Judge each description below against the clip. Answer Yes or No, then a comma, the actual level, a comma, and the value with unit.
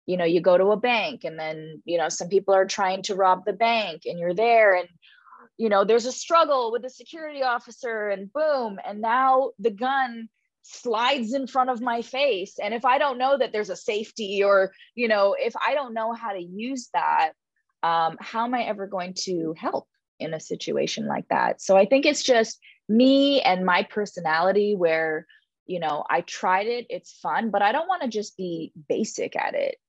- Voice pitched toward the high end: Yes, high, 225 Hz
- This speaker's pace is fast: Yes, fast, 210 wpm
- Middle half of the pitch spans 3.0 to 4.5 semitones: No, wide, 5.4 semitones